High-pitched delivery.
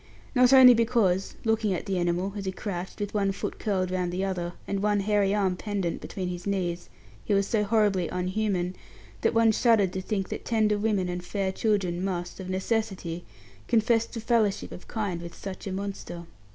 Yes: high, 195 Hz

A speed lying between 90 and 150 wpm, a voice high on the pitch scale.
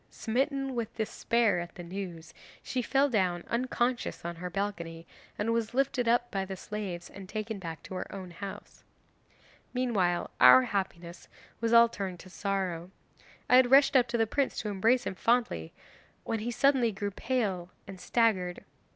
No: average, 170 wpm; high, 205 Hz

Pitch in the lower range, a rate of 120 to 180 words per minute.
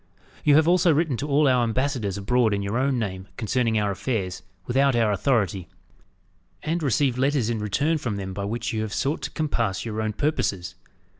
No: low, 120 Hz; average, 195 wpm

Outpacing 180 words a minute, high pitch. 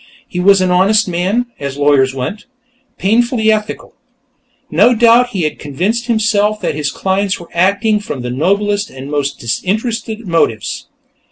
No: average, 150 wpm; high, 195 Hz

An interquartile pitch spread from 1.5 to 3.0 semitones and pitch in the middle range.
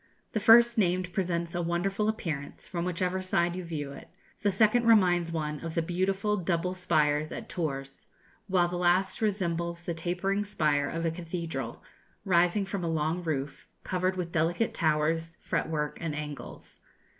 Yes: narrow, 2.5 semitones; medium, 175 Hz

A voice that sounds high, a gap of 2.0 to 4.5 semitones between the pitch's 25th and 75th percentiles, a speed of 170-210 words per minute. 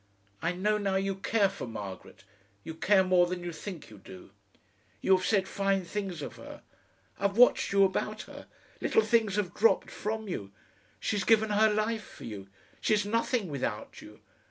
Yes: high, 195 Hz; average, 3.3 semitones; average, 180 wpm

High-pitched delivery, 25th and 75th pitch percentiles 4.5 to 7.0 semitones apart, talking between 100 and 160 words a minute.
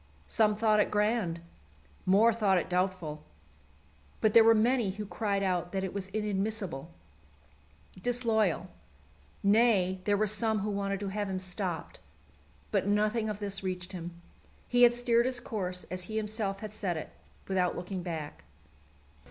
No: high, 200 Hz; average, 2.8 semitones; average, 155 wpm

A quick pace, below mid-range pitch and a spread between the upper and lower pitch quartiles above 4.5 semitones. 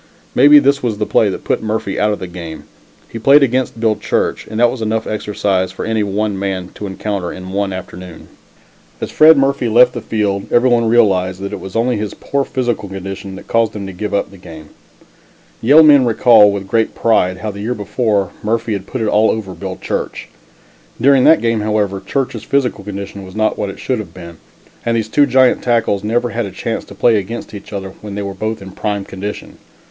No: fast, 215 wpm; low, 105 Hz; average, 3.2 semitones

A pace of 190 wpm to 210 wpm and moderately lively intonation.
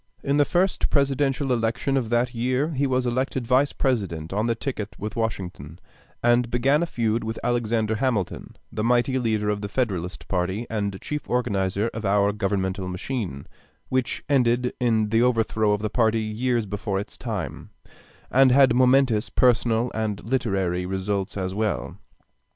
No: average, 160 wpm; average, 3.8 semitones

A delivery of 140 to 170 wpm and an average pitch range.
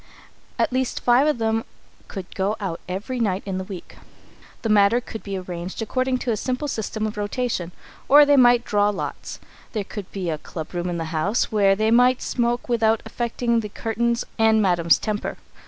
No: average, 190 wpm; average, 3.8 semitones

